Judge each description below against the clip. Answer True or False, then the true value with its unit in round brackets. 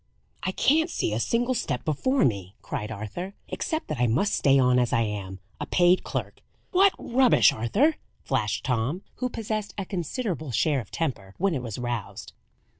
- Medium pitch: True (150 Hz)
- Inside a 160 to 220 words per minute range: True (180 wpm)